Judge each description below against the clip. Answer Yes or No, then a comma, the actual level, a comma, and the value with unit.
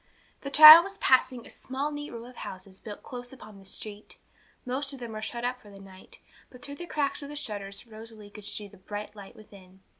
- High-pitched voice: Yes, high, 230 Hz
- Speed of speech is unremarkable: No, fast, 230 wpm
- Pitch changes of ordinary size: Yes, average, 4.8 semitones